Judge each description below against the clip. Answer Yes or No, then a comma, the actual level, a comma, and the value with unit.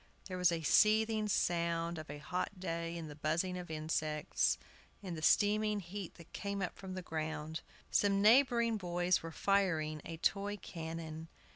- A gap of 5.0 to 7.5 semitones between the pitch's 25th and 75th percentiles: No, average, 3.7 semitones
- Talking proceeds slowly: No, average, 165 wpm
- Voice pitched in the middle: Yes, medium, 175 Hz